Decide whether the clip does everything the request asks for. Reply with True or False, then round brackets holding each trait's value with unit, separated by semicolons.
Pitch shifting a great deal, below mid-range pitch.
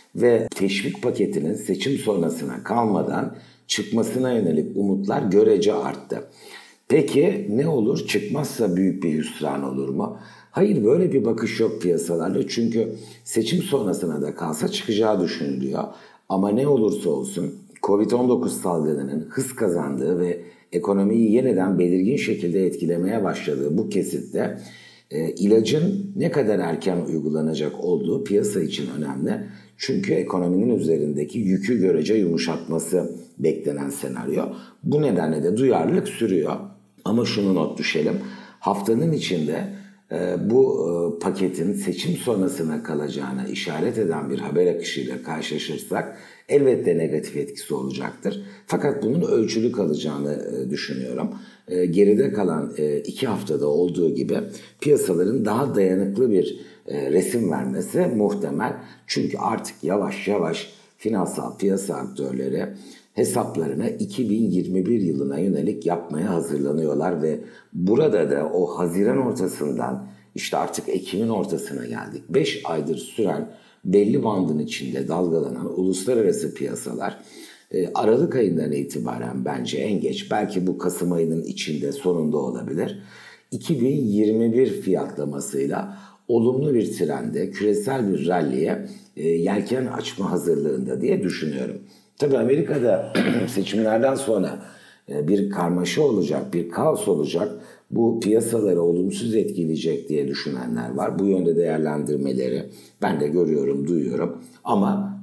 True (7.3 semitones; 95 Hz)